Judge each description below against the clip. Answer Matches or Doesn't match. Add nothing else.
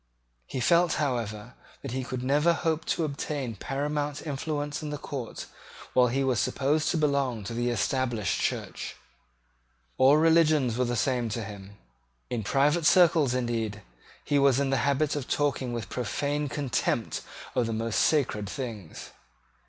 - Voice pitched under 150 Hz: Matches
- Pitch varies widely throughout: Doesn't match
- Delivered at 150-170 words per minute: Matches